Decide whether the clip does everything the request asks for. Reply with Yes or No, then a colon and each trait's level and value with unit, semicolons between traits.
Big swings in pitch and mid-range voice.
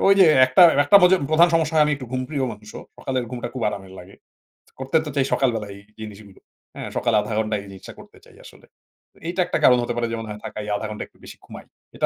No: wide, 5.7 semitones; low, 120 Hz